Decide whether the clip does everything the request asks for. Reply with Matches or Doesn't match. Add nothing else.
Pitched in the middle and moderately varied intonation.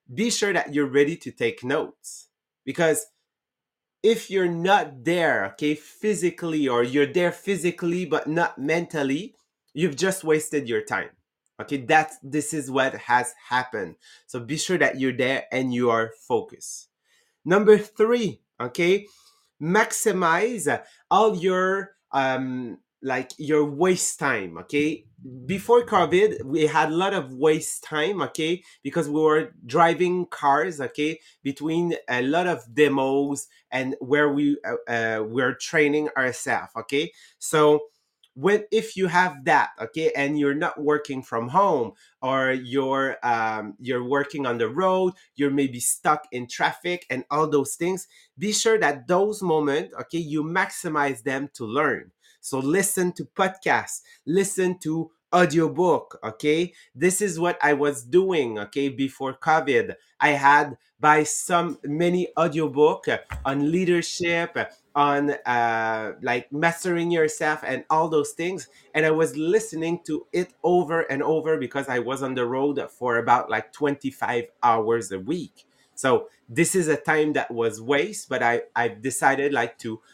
Matches